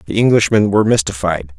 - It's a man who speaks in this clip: Yes, male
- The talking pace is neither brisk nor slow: Yes, average, 150 wpm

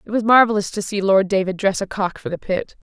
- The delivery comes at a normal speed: No, fast, 265 wpm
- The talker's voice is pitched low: No, high, 200 Hz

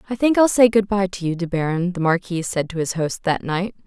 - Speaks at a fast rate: Yes, fast, 280 wpm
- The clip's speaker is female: Yes, female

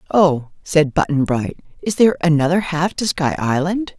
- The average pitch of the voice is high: No, medium, 165 Hz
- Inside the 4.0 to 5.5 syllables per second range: Yes, 4.8 syllables/s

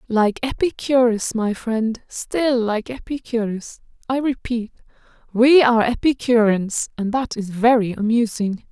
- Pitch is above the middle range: Yes, high, 230 Hz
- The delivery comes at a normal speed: No, slow, 115 wpm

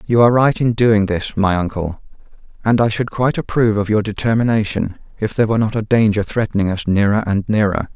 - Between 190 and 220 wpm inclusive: Yes, fast, 205 wpm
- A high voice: No, low, 105 Hz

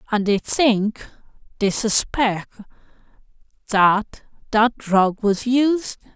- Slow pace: Yes, slow, 80 wpm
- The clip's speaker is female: Yes, female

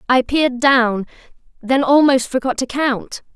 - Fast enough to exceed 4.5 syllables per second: No, 4.4 syllables/s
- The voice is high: Yes, very high, 260 Hz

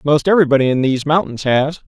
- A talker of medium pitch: Yes, medium, 145 Hz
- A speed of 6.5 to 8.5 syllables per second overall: Yes, 6.9 syllables/s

